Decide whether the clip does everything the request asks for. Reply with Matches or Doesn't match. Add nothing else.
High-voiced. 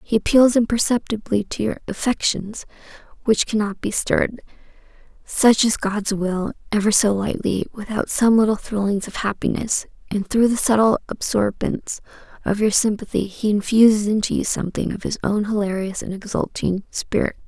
Matches